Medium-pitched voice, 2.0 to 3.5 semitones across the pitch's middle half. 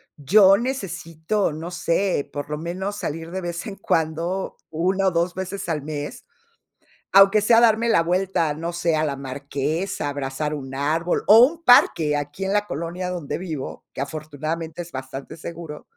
No: medium, 165 Hz; average, 4.2 semitones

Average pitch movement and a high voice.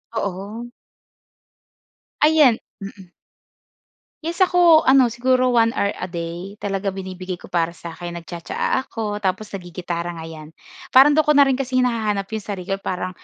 No: wide, 6.0 semitones; high, 200 Hz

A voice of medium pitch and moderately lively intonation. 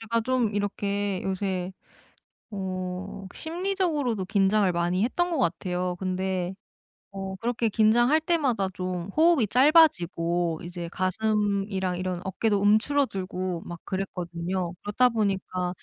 No: high, 195 Hz; average, 3.9 semitones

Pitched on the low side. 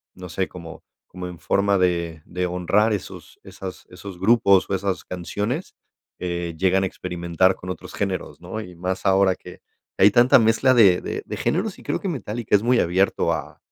Yes: very low, 95 Hz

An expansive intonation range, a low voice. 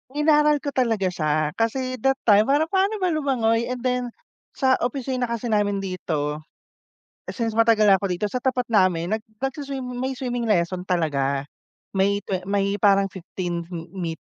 No: wide, 5.7 semitones; high, 225 Hz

